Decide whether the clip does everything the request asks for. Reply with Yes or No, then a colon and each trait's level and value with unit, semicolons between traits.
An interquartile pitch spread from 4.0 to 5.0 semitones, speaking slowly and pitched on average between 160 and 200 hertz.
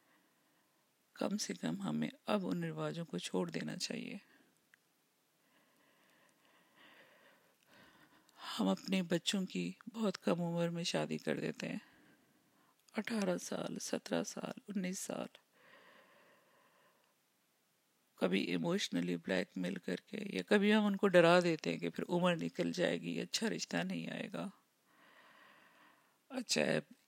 Yes: average, 4.3 semitones; slow, 70 wpm; medium, 185 Hz